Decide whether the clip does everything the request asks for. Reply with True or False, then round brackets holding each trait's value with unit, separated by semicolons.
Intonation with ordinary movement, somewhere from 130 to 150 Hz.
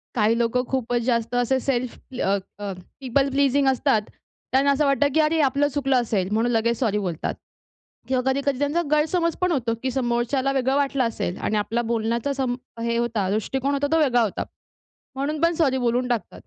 False (3.1 semitones; 255 Hz)